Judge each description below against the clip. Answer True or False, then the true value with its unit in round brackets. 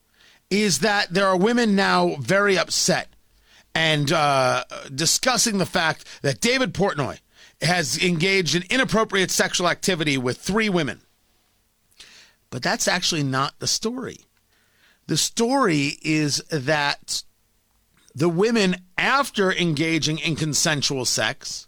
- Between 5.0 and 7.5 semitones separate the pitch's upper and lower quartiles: True (5.6 semitones)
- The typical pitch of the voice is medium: True (175 Hz)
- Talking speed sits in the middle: False (115 wpm)